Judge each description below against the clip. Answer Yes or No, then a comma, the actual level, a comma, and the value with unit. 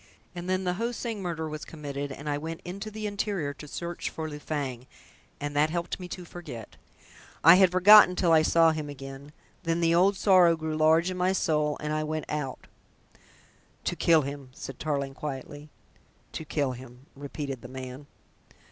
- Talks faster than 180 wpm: Yes, average, 190 wpm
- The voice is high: No, medium, 155 Hz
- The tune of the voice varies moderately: Yes, average, 3.7 semitones